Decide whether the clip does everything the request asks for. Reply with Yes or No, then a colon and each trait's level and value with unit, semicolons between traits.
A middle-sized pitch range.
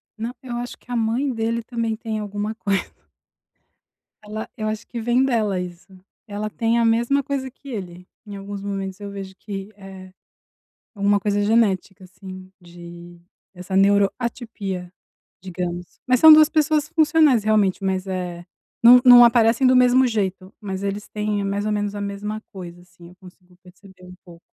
Yes: average, 3.7 semitones